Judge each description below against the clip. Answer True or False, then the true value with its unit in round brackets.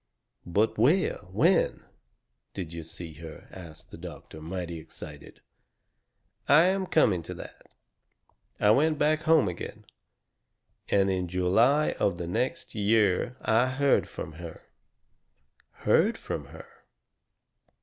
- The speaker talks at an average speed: False (120 wpm)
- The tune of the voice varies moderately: False (8.6 semitones)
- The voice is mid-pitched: False (100 Hz)